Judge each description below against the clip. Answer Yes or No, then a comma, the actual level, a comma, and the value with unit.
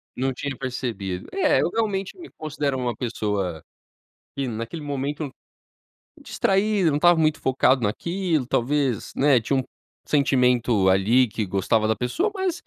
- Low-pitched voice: Yes, low, 130 Hz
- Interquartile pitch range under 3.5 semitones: No, average, 5.3 semitones